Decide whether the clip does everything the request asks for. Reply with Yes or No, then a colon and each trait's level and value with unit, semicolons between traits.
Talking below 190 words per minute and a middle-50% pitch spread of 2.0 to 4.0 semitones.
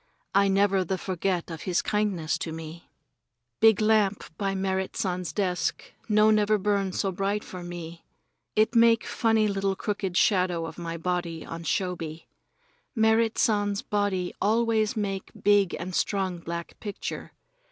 Yes: average, 145 wpm; average, 2.9 semitones